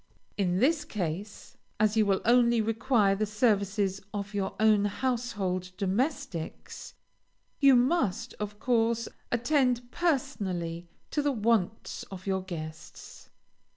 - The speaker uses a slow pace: Yes, slow, 120 wpm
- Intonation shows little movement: No, average, 4.1 semitones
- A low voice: No, high, 215 Hz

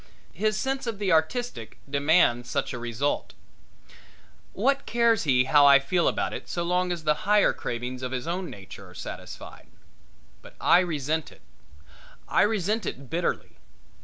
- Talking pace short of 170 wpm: Yes, average, 160 wpm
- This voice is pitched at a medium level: Yes, medium, 165 Hz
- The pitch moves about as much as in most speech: No, wide, 7.1 semitones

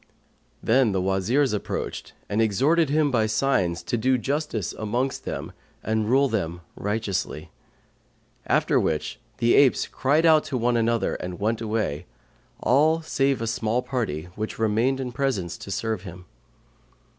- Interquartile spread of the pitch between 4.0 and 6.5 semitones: Yes, average, 4.6 semitones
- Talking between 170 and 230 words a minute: No, average, 145 wpm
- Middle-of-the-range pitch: No, low, 115 Hz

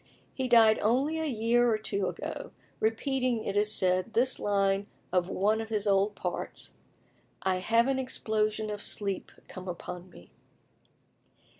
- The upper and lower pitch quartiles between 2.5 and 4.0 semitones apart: Yes, average, 3.0 semitones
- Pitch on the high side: Yes, high, 215 Hz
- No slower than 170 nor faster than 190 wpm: No, average, 150 wpm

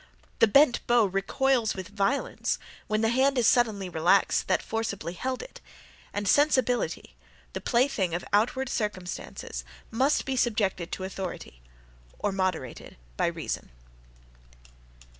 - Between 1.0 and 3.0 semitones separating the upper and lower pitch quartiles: No, average, 5.0 semitones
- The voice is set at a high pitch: Yes, high, 215 Hz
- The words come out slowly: Yes, slow, 125 wpm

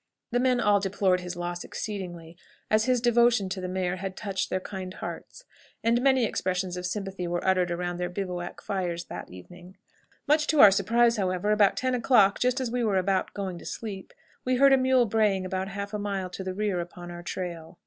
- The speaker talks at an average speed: No, fast, 210 wpm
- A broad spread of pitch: No, average, 3.8 semitones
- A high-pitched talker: Yes, high, 195 Hz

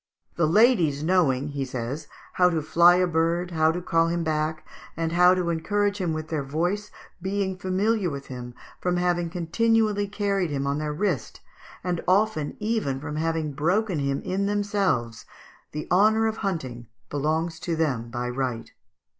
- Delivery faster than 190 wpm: No, average, 165 wpm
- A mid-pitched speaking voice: Yes, medium, 165 Hz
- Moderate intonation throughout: Yes, average, 4.3 semitones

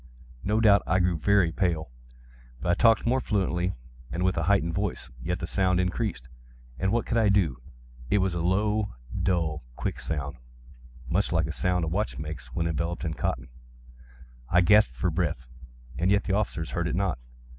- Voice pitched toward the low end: Yes, very low, 85 Hz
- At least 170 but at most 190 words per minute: Yes, average, 175 wpm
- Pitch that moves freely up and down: Yes, wide, 6.5 semitones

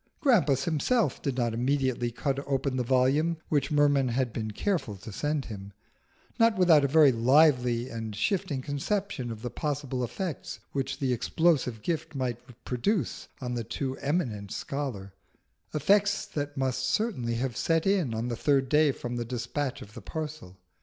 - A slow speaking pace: No, average, 165 wpm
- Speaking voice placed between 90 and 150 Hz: Yes, low, 135 Hz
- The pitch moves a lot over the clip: No, average, 4.1 semitones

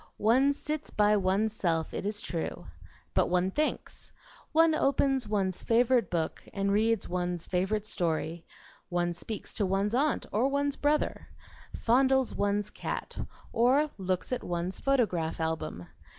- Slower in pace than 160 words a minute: Yes, average, 140 wpm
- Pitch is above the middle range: Yes, high, 210 Hz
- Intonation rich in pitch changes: Yes, wide, 6.5 semitones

